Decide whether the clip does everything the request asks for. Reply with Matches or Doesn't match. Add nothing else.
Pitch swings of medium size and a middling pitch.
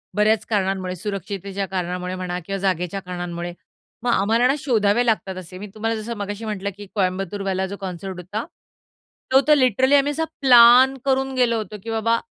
Doesn't match